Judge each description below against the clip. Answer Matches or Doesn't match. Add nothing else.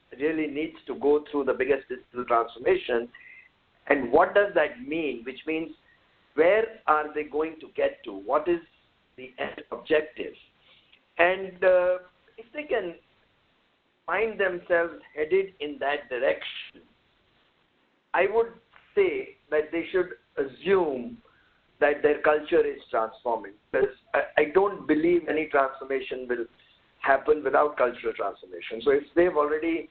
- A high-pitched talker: Doesn't match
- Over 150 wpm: Doesn't match